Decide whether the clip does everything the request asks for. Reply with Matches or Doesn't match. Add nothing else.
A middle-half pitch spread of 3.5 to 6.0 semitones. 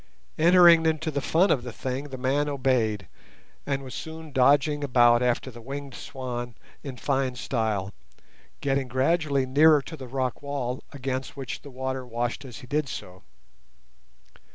Doesn't match